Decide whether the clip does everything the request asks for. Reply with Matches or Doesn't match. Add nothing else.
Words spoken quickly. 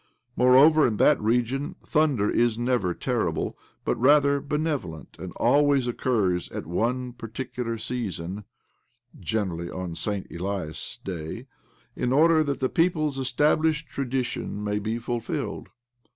Doesn't match